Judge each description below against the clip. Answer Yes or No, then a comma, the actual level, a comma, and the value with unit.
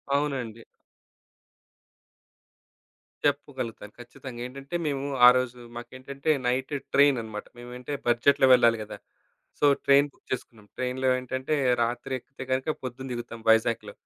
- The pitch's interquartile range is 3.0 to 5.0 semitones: No, narrow, 2.4 semitones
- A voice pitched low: Yes, low, 130 Hz